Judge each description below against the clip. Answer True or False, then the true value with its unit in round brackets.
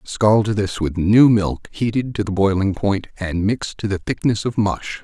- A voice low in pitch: True (100 Hz)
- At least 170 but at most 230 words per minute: True (200 wpm)